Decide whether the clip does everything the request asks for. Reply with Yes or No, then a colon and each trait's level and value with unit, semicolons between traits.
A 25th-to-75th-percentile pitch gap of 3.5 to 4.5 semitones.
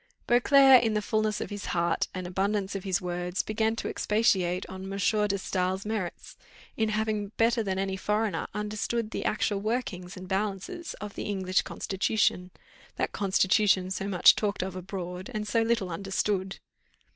No: narrow, 2.4 semitones